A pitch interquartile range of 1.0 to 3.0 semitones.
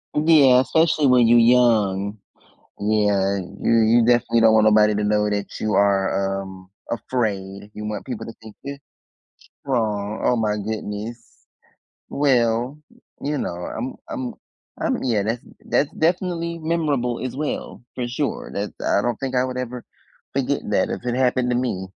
No: average, 3.7 semitones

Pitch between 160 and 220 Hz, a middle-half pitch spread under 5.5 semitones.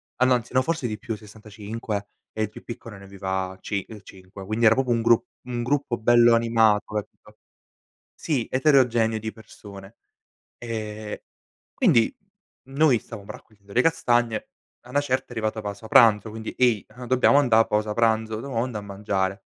No: low, 110 Hz; narrow, 2.5 semitones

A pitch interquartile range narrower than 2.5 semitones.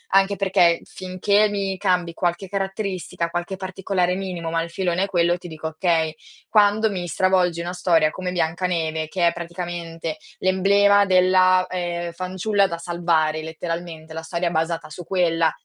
Yes: narrow, 2.0 semitones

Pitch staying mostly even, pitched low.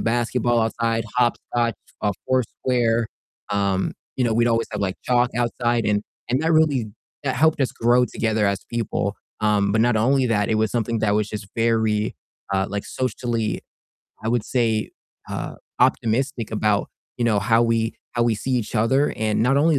Yes: narrow, 2.2 semitones; low, 115 Hz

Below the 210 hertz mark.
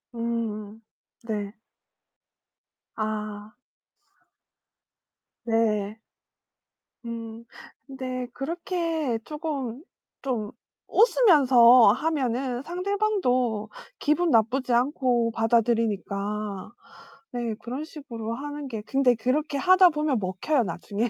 No: high, 245 Hz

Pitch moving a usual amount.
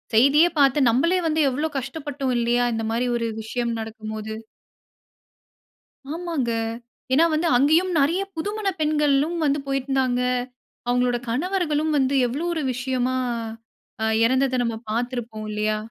Yes: average, 4.1 semitones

